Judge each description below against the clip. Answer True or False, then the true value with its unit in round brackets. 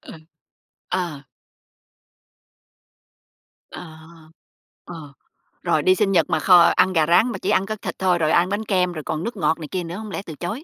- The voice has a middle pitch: True (180 Hz)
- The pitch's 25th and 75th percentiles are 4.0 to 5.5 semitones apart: False (3.2 semitones)